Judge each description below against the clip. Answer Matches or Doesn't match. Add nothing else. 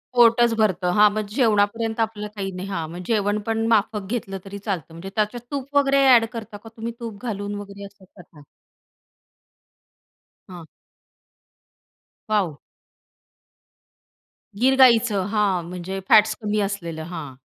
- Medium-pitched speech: Doesn't match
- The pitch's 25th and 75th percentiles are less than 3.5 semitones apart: Matches